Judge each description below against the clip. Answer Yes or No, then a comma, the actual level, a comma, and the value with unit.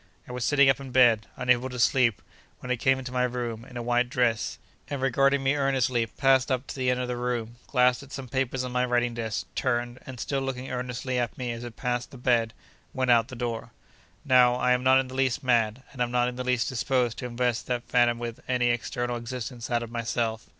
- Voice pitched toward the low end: Yes, low, 125 Hz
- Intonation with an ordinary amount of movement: No, narrow, 1.4 semitones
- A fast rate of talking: Yes, fast, 240 wpm